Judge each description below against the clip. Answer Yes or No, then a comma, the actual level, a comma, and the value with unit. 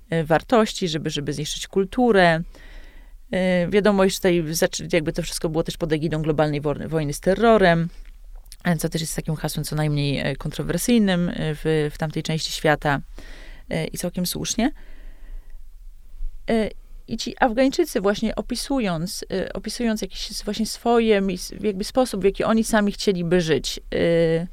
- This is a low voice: No, medium, 180 Hz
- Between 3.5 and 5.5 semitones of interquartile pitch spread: Yes, average, 4.8 semitones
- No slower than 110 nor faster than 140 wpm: Yes, average, 130 wpm